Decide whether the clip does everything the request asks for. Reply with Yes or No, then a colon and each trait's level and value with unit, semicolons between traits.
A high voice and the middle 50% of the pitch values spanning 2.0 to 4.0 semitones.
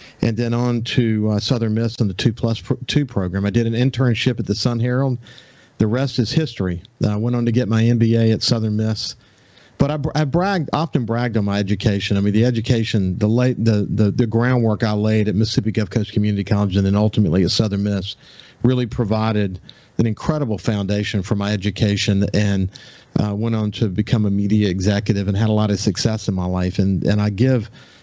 No: low, 110 Hz; average, 2.9 semitones